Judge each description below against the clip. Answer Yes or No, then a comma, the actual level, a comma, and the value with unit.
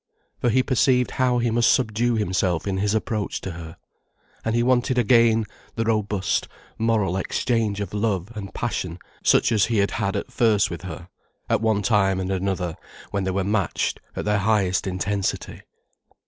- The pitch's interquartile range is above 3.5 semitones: No, average, 3.2 semitones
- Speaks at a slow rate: No, average, 175 wpm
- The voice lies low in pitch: Yes, low, 105 Hz